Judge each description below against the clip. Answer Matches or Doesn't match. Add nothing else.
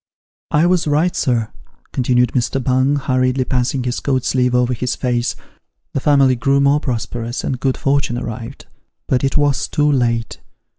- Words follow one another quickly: Doesn't match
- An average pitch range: Doesn't match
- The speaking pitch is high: Doesn't match